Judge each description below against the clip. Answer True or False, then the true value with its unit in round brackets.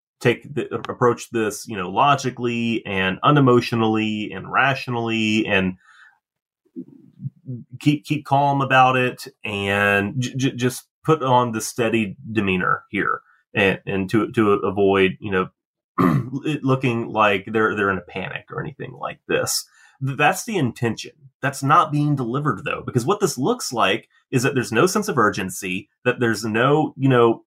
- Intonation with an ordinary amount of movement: True (4.0 semitones)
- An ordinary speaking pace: True (155 wpm)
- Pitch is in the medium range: False (120 Hz)